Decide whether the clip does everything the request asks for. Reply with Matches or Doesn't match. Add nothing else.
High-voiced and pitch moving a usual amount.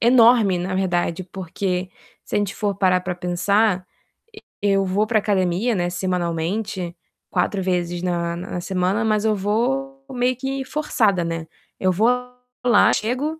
Matches